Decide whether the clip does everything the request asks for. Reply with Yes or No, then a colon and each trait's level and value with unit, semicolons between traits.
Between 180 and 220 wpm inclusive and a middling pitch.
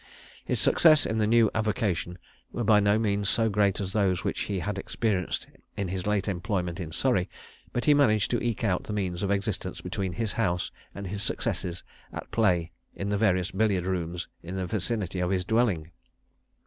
No: average, 190 wpm; low, 100 Hz